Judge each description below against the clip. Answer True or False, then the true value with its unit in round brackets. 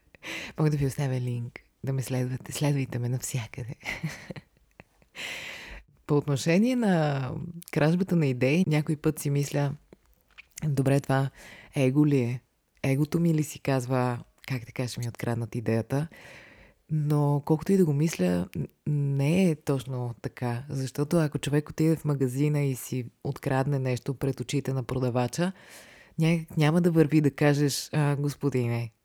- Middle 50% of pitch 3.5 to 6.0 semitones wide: False (3.1 semitones)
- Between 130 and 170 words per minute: True (140 wpm)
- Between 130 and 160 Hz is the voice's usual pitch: True (140 Hz)